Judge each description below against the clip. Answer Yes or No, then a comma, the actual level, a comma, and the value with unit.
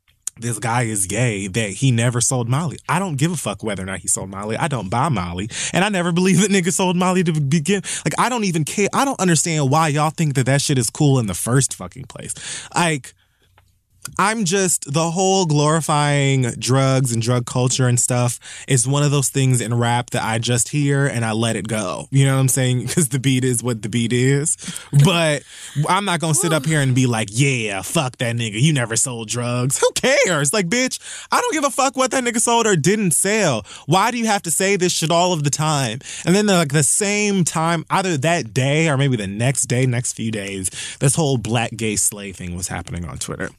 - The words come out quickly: Yes, fast, 235 wpm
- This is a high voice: No, medium, 140 Hz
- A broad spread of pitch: Yes, wide, 6.3 semitones